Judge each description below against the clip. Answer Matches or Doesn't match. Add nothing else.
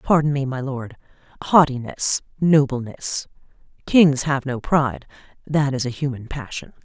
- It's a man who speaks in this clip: Doesn't match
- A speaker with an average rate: Doesn't match